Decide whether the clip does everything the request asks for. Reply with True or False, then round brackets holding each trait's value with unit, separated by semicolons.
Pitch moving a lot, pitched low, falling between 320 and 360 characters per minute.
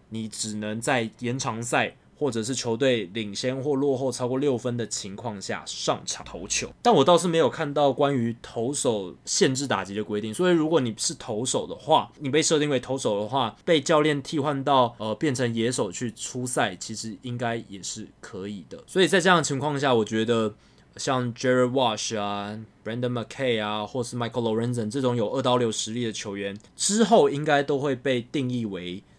False (4.3 semitones; 125 Hz; 335 characters per minute)